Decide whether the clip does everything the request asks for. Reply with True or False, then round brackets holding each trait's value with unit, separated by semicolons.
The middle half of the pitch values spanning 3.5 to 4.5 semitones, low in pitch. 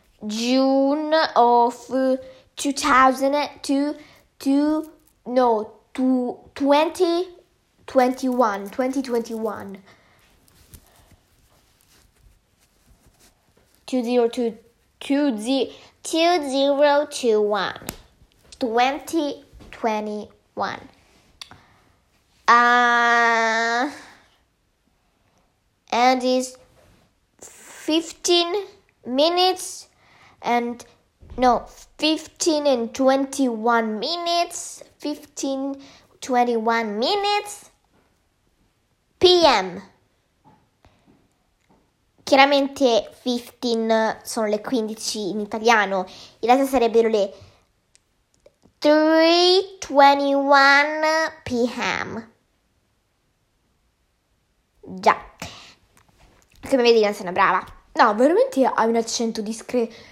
False (4.2 semitones; 255 Hz)